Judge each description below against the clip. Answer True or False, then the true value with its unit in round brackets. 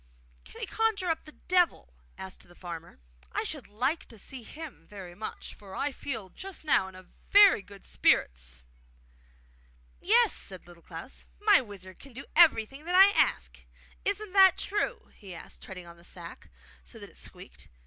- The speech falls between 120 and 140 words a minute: False (170 wpm)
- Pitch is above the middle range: True (225 Hz)